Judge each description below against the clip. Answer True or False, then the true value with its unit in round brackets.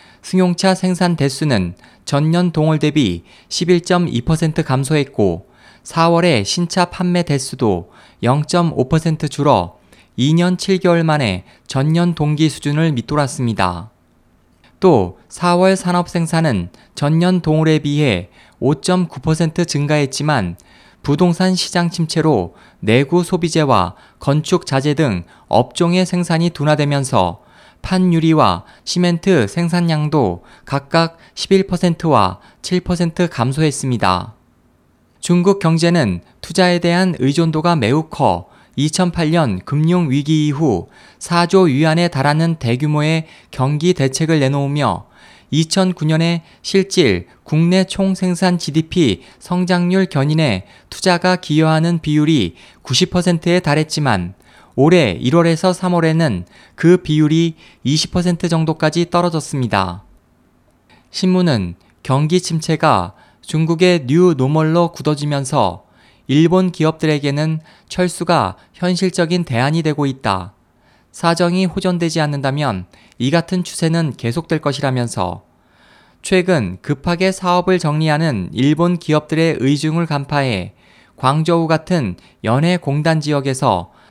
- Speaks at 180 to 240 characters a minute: True (230 characters per minute)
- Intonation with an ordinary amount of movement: True (5.0 semitones)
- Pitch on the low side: False (155 Hz)